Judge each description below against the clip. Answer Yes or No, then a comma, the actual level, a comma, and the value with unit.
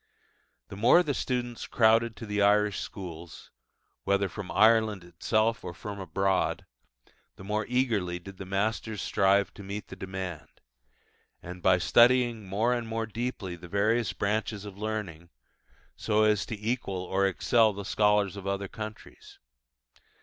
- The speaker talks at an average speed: Yes, average, 145 wpm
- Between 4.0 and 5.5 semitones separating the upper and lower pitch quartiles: No, narrow, 2.5 semitones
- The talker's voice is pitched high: No, low, 105 Hz